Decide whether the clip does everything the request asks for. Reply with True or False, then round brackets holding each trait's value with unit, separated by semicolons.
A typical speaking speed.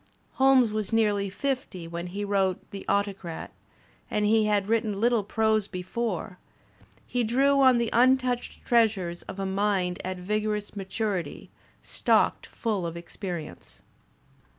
False (130 wpm)